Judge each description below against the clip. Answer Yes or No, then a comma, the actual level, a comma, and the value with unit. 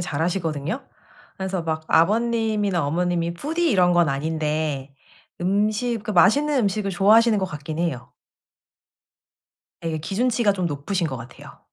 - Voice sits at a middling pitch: Yes, medium, 180 Hz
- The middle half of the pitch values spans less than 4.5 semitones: No, average, 5.1 semitones